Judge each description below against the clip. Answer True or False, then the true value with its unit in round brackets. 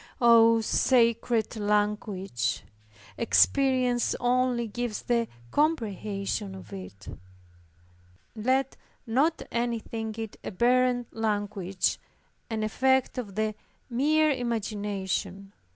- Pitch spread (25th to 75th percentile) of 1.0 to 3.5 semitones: True (3.2 semitones)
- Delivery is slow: True (90 wpm)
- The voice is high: True (225 Hz)